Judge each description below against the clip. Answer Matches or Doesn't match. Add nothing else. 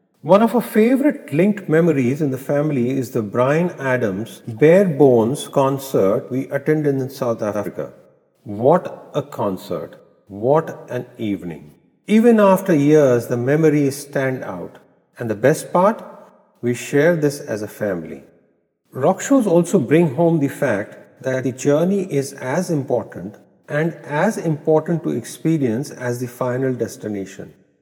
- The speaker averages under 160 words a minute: Matches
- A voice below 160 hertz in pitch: Matches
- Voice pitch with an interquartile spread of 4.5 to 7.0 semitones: Matches